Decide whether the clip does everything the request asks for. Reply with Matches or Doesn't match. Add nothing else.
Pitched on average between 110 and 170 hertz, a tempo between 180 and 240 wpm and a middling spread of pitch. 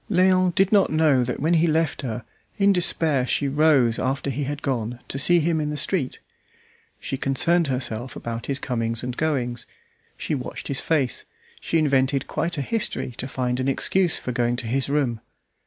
Matches